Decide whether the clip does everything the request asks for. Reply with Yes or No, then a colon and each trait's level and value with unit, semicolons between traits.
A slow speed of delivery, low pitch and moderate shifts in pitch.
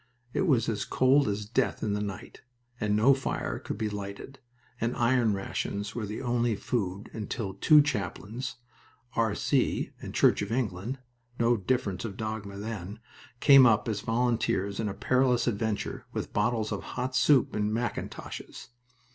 No: average, 160 wpm; low, 110 Hz; average, 3.2 semitones